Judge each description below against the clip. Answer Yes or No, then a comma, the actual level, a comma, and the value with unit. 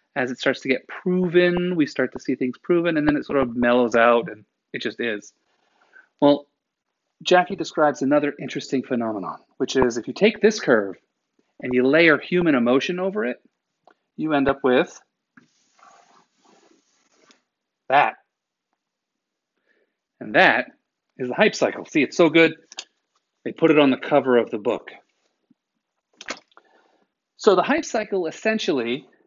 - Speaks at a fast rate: No, average, 150 wpm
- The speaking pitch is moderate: Yes, medium, 150 Hz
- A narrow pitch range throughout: No, wide, 5.5 semitones